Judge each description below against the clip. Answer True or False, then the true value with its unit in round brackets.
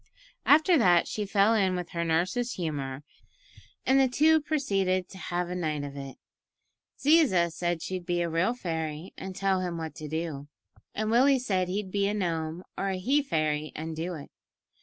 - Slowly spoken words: False (185 wpm)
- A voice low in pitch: False (180 Hz)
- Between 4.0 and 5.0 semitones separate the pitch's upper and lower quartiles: True (4.5 semitones)